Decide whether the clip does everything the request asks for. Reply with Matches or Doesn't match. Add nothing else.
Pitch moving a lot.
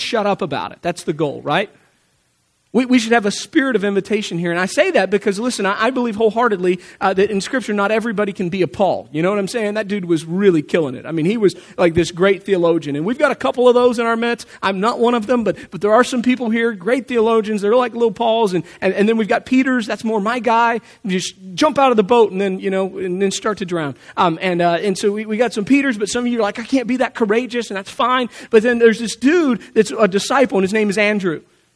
Doesn't match